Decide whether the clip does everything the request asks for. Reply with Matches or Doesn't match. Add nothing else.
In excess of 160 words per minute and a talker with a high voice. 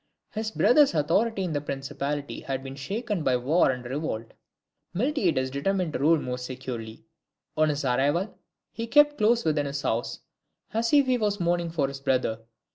Doesn't match